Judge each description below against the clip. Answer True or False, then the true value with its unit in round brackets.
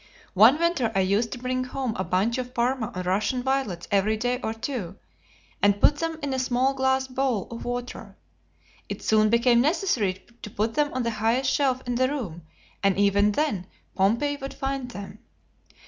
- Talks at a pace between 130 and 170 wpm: False (185 wpm)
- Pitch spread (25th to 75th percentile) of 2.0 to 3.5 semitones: False (4.4 semitones)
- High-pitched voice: True (245 Hz)